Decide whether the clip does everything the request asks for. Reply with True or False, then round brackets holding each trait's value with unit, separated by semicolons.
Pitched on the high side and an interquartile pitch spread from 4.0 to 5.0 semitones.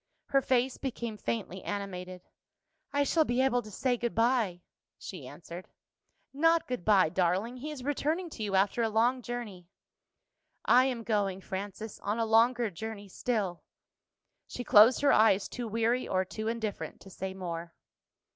True (220 Hz; 4.4 semitones)